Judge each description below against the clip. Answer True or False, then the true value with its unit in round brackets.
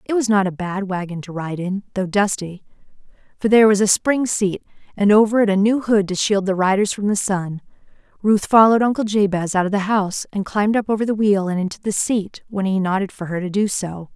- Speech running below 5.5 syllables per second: False (5.8 syllables/s)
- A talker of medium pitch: False (200 Hz)